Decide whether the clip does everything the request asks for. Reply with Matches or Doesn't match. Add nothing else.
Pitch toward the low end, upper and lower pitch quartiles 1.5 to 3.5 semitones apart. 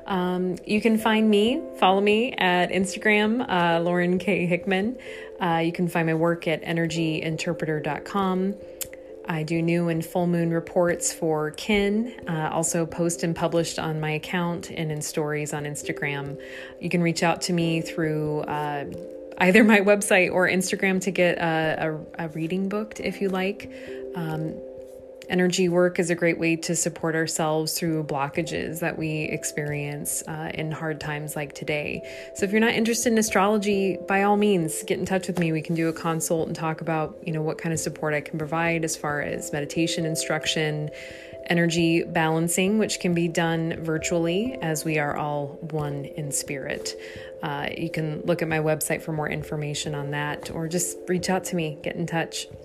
Doesn't match